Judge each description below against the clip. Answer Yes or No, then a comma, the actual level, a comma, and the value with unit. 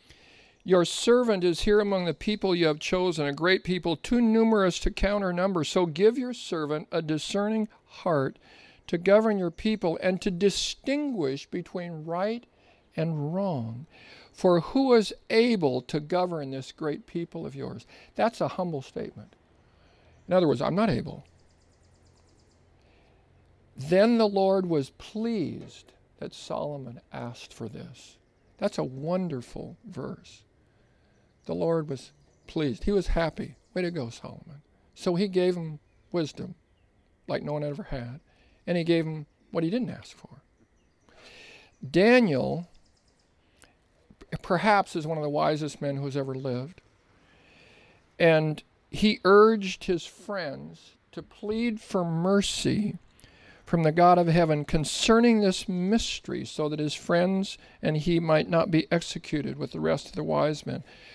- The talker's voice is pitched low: No, medium, 170 Hz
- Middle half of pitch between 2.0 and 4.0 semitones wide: No, average, 5.2 semitones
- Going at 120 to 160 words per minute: Yes, average, 145 wpm